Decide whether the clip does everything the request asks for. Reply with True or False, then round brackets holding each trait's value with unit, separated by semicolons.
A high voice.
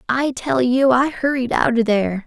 True (250 Hz)